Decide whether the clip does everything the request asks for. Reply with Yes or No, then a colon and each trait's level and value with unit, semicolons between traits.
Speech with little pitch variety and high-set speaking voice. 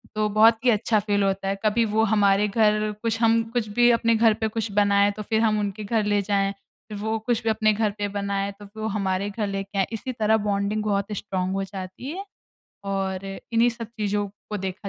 Yes: narrow, 1.9 semitones; high, 210 Hz